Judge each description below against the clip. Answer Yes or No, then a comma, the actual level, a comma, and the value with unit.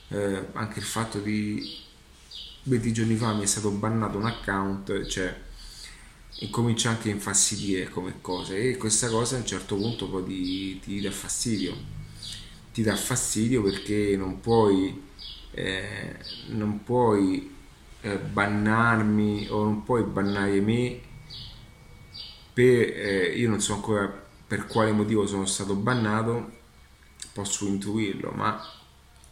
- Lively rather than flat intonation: No, narrow, 2.6 semitones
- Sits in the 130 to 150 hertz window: No, low, 105 Hz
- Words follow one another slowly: No, average, 130 wpm